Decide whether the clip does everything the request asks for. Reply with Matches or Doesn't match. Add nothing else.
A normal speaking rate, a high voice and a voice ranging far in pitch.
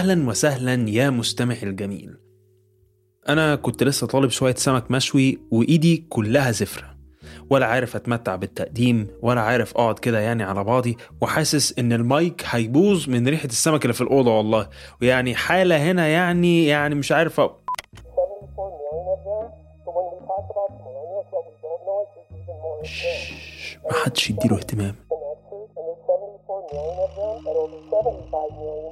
Doesn't match